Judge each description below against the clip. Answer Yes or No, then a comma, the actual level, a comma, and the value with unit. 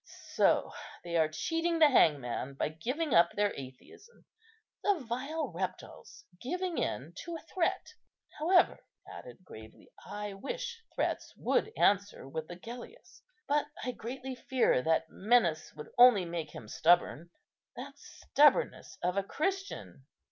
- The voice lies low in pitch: No, high, 230 Hz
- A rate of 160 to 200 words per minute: No, slow, 135 wpm